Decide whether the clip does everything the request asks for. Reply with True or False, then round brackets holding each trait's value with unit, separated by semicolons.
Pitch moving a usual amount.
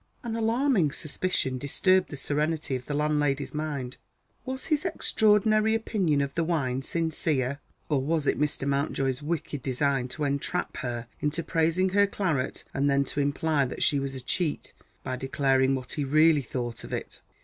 True (3.7 semitones)